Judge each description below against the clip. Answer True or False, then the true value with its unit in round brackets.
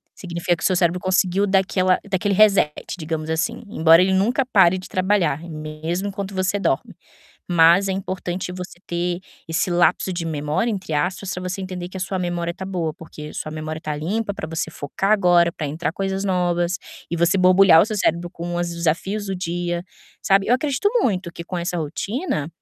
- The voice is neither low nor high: True (180 Hz)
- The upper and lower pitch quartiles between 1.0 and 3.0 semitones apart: True (2.5 semitones)